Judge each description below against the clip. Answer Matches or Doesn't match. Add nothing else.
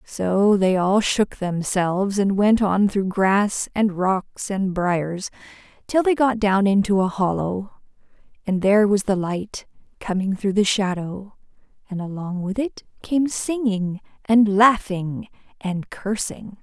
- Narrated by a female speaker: Matches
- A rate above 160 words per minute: Doesn't match